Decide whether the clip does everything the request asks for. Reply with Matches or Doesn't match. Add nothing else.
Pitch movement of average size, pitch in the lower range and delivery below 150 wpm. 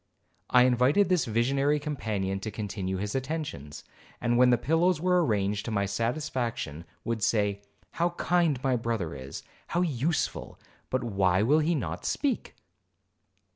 Doesn't match